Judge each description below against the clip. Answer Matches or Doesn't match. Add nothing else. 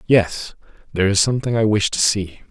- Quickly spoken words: Doesn't match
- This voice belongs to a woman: Doesn't match